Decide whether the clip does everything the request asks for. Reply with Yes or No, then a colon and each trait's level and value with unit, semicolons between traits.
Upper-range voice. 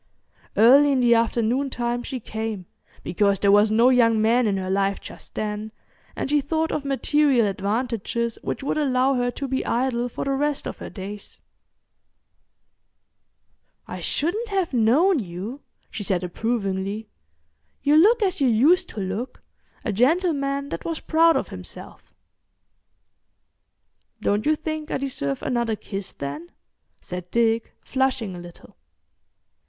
Yes: high, 240 Hz